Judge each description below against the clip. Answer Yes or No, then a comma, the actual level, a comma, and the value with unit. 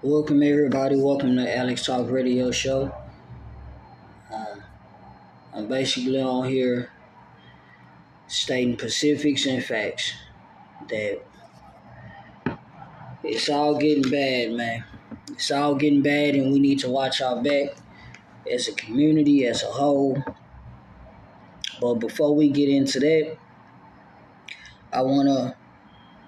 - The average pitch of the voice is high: No, low, 135 Hz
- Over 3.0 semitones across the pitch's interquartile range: No, average, 2.7 semitones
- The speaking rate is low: Yes, slow, 110 wpm